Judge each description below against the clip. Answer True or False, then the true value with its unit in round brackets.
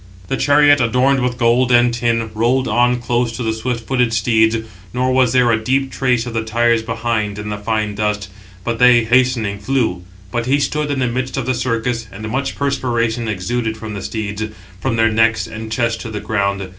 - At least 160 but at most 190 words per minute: False (205 wpm)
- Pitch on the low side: True (115 Hz)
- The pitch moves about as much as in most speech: False (2.2 semitones)